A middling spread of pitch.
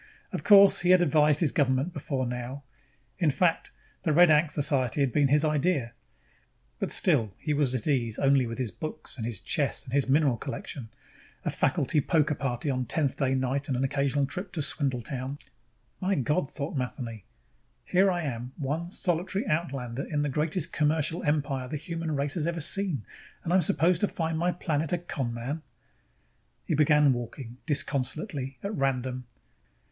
Yes: average, 3.7 semitones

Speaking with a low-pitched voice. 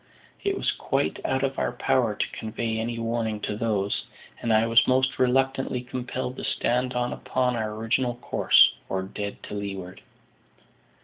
Yes: low, 115 Hz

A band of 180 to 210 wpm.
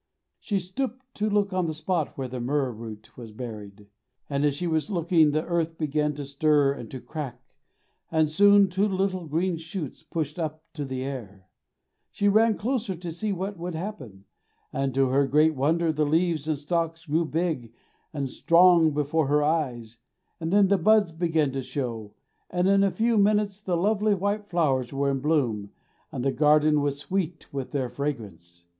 Yes: average, 185 wpm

